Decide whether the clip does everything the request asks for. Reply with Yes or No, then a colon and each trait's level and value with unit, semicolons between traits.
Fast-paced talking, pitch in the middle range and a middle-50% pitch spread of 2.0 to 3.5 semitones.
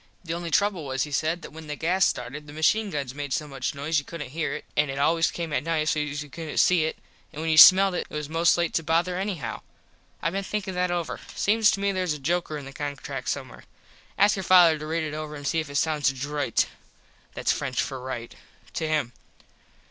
Yes: fast, 240 wpm; medium, 155 Hz; average, 3.1 semitones